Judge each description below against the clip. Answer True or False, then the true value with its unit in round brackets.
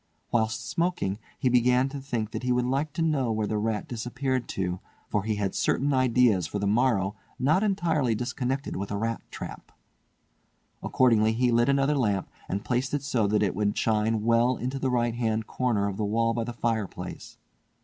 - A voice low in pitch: True (120 Hz)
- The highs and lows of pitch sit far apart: False (3.3 semitones)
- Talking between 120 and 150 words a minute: False (190 wpm)